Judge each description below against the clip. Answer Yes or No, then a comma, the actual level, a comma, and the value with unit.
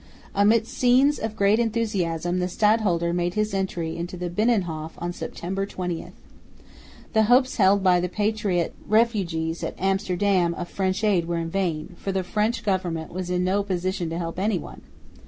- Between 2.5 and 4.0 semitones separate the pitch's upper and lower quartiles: Yes, average, 3.3 semitones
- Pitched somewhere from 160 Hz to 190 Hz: Yes, medium, 185 Hz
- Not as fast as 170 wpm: Yes, average, 160 wpm